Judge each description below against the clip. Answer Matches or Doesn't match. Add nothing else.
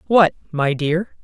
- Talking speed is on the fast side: Doesn't match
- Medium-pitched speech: Matches